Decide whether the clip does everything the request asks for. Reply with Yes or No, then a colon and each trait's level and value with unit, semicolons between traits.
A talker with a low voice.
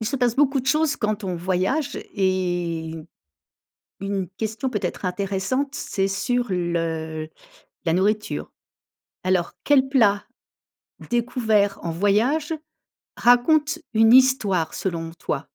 No: high, 205 Hz